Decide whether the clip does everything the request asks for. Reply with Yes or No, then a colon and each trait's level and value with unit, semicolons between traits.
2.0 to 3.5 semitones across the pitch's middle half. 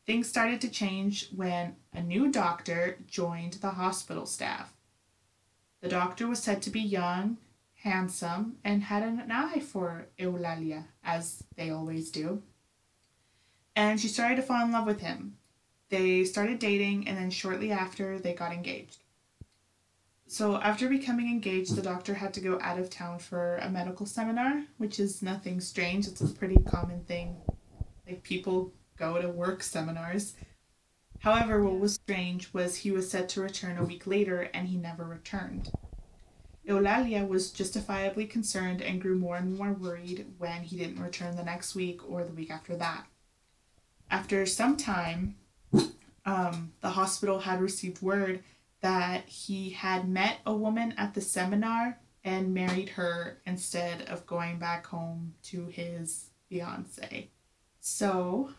Yes: average, 2.8 semitones